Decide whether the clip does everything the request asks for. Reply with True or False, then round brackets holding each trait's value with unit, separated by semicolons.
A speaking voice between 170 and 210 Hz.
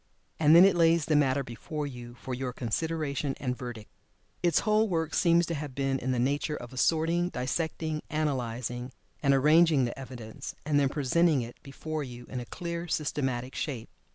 False (140 Hz)